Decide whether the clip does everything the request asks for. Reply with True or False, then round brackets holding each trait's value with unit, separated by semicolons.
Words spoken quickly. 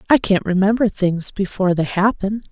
False (165 wpm)